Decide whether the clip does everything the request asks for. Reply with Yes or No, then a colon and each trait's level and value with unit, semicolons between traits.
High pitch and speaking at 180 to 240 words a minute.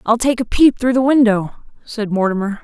Yes: high, 230 Hz; fast, 205 wpm